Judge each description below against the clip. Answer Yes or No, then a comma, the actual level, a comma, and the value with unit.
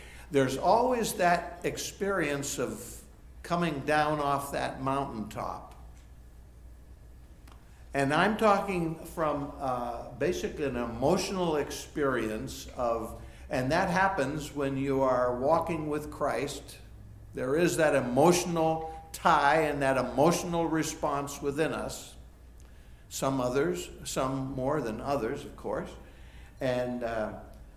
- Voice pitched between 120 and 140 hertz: Yes, low, 135 Hz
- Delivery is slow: Yes, slow, 110 wpm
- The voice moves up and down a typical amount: No, wide, 6.7 semitones